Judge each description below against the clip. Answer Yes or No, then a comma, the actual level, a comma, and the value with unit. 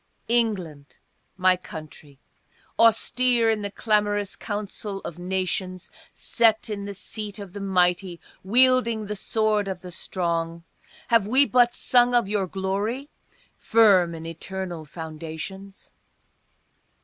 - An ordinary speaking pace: No, slow, 120 wpm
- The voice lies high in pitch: Yes, high, 200 Hz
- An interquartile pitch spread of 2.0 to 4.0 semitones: Yes, average, 3.7 semitones